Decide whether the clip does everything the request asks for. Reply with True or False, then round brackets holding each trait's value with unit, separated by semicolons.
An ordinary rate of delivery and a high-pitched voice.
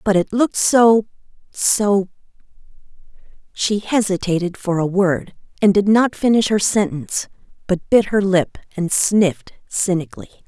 False (125 wpm; 195 Hz)